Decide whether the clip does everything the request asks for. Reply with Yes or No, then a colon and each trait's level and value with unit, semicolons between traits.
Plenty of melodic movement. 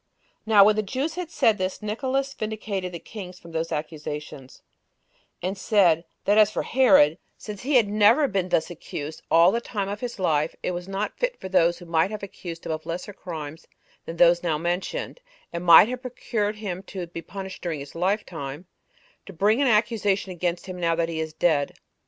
No: average, 4.2 semitones